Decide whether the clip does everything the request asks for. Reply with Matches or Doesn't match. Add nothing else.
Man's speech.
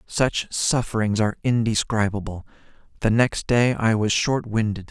Matches